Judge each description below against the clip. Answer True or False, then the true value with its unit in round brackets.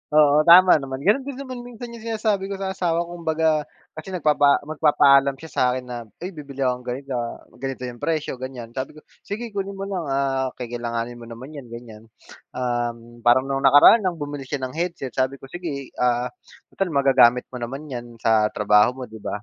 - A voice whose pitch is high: False (135 Hz)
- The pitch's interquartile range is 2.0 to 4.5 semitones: False (5.5 semitones)